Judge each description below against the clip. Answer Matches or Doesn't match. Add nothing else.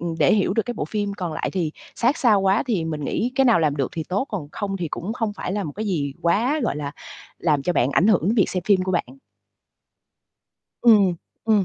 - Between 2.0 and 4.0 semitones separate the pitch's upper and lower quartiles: Doesn't match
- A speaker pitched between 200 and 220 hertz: Doesn't match